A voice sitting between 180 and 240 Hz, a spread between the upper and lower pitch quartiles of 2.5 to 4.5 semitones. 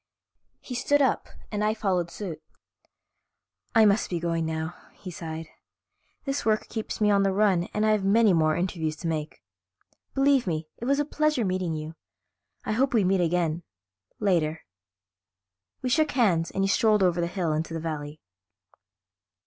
No: medium, 185 Hz; average, 4.9 semitones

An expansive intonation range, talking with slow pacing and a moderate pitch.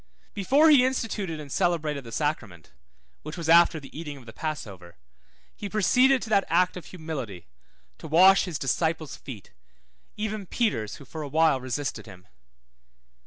No: wide, 6.2 semitones; average, 160 wpm; medium, 160 Hz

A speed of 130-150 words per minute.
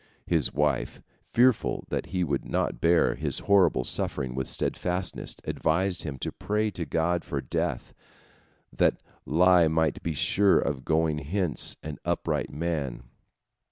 Yes: average, 145 wpm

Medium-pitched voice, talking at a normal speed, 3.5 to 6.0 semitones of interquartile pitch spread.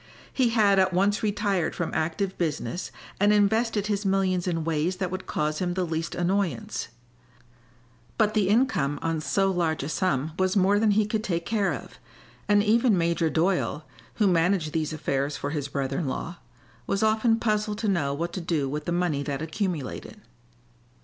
Yes: medium, 180 Hz; average, 180 wpm; average, 4.4 semitones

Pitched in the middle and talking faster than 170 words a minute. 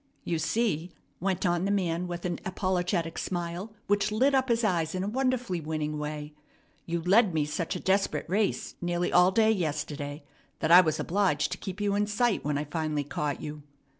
Yes: medium, 175 Hz; average, 195 wpm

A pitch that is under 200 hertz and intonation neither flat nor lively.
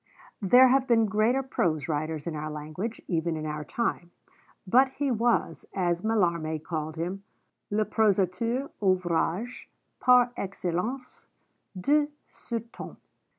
No: high, 190 Hz; wide, 6.4 semitones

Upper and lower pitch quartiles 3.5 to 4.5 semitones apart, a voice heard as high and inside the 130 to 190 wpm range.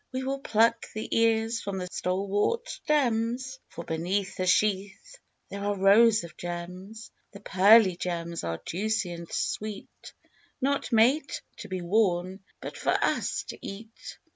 Yes: average, 3.8 semitones; high, 205 Hz; average, 145 wpm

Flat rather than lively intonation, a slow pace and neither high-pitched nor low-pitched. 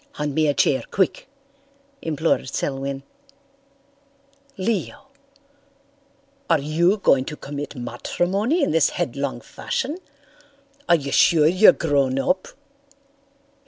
No: average, 5.1 semitones; slow, 105 wpm; medium, 155 Hz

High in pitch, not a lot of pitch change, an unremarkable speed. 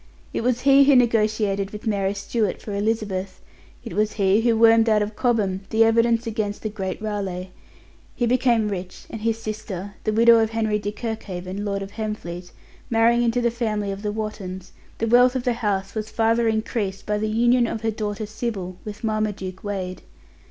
Yes: high, 215 Hz; narrow, 2.3 semitones; average, 185 wpm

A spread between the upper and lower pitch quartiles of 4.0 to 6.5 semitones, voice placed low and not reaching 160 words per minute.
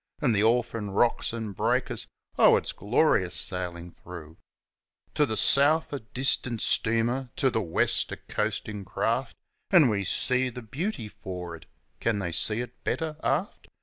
Yes: average, 4.6 semitones; low, 115 Hz; average, 150 wpm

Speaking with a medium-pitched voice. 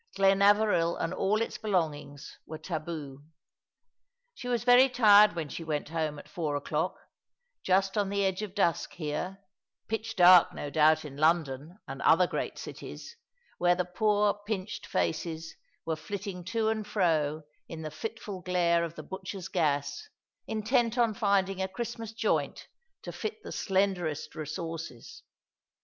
Yes: medium, 180 Hz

